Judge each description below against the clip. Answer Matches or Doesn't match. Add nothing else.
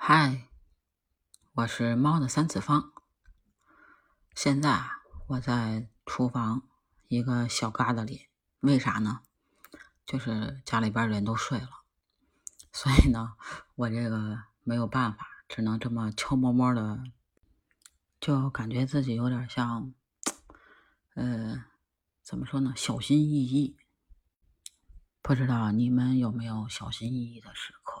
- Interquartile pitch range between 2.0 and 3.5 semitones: Matches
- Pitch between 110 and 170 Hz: Matches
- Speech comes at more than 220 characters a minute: Doesn't match